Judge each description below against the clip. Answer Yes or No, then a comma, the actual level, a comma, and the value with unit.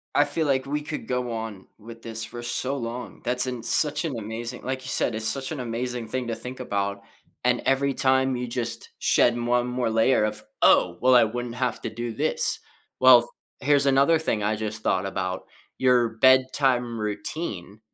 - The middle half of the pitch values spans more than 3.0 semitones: No, average, 2.7 semitones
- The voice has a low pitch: Yes, low, 120 Hz